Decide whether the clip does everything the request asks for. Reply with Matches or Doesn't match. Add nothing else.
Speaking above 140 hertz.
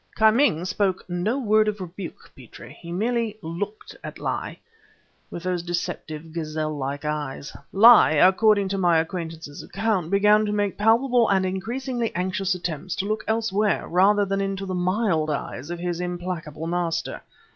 Matches